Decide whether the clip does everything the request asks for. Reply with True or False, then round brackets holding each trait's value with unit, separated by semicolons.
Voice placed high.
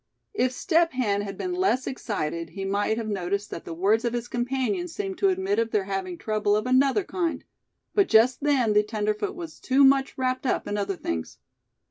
True (235 Hz)